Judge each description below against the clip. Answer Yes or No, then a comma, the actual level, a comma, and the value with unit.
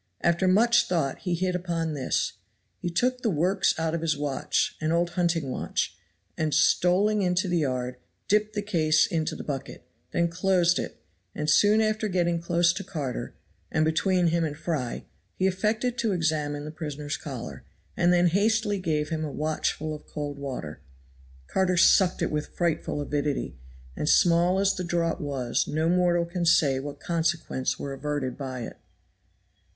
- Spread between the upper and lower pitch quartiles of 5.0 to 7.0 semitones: No, average, 3.5 semitones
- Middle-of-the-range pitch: Yes, medium, 165 Hz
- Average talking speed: Yes, average, 170 wpm